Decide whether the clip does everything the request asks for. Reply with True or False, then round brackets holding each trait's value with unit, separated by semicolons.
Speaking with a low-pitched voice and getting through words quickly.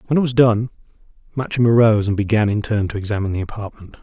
True (110 Hz; 210 wpm)